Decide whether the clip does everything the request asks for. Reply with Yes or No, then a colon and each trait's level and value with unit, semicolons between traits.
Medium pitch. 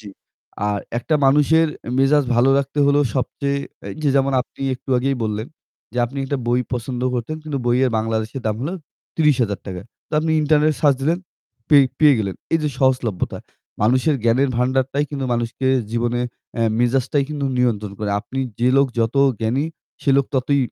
No: low, 130 Hz